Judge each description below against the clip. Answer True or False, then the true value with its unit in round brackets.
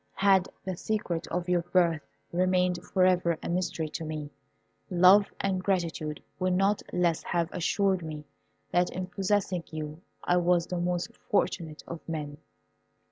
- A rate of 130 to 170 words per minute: True (150 wpm)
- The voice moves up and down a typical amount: False (2.0 semitones)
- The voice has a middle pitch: True (180 Hz)